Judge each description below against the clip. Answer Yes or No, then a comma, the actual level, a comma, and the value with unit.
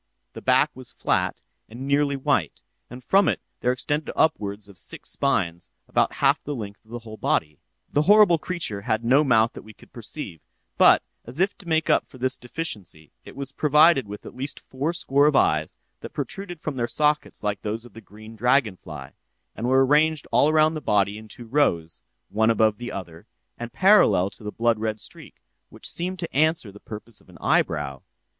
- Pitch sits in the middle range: No, low, 120 Hz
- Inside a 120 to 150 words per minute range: No, average, 200 wpm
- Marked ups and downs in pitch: Yes, wide, 6.1 semitones